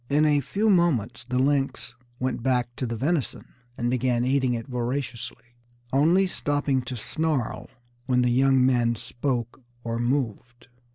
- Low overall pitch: Yes, low, 130 Hz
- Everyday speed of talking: Yes, average, 150 wpm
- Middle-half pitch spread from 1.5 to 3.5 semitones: Yes, average, 2.7 semitones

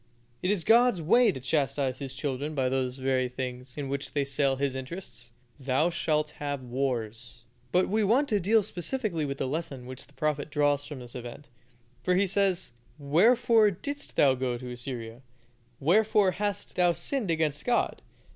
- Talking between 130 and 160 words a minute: No, average, 175 wpm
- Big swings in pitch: Yes, wide, 6.2 semitones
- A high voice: No, medium, 145 Hz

